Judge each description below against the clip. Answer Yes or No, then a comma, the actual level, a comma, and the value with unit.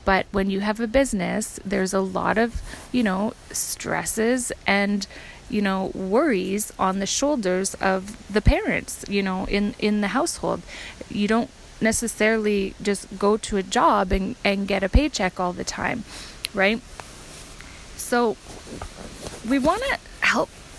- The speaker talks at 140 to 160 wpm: Yes, average, 145 wpm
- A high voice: Yes, high, 205 Hz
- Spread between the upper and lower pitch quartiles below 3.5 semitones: Yes, average, 2.8 semitones